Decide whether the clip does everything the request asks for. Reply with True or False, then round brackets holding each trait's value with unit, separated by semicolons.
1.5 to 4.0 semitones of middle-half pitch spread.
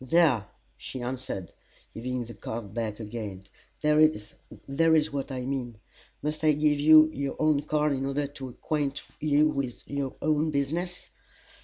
True (3.5 semitones)